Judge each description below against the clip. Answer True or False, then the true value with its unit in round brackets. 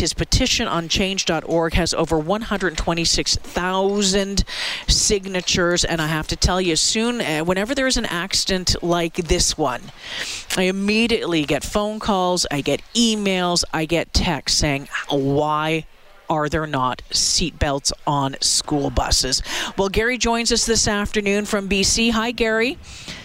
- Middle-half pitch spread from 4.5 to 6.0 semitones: True (4.9 semitones)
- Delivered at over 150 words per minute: False (135 wpm)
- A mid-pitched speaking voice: True (180 Hz)